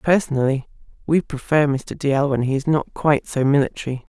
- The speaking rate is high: No, average, 175 wpm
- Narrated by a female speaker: Yes, female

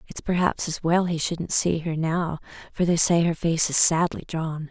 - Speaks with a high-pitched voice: No, medium, 165 Hz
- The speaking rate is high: Yes, fast, 215 wpm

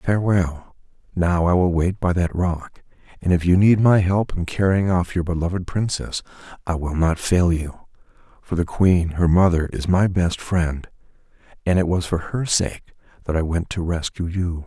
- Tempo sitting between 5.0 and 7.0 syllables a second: No, 4.6 syllables/s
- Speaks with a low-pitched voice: Yes, very low, 90 Hz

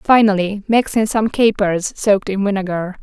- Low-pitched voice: No, high, 205 Hz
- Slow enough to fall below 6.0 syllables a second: Yes, 4.8 syllables/s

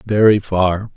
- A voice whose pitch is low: Yes, low, 100 Hz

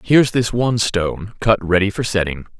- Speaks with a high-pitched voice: No, low, 105 Hz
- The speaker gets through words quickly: No, average, 185 wpm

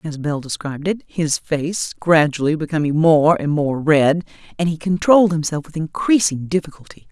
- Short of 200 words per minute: Yes, average, 160 wpm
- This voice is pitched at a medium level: Yes, medium, 160 Hz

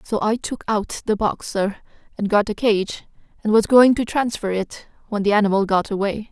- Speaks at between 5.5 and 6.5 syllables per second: No, 5.0 syllables/s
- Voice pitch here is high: Yes, high, 210 Hz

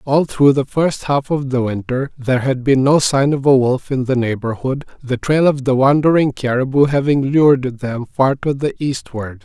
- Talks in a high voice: No, low, 135 Hz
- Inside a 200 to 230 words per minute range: Yes, fast, 205 wpm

